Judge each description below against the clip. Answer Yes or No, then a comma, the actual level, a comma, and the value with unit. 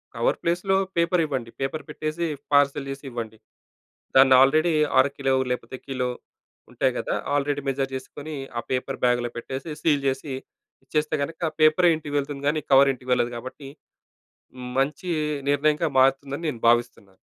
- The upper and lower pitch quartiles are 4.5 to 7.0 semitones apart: No, average, 2.8 semitones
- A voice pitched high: No, medium, 140 Hz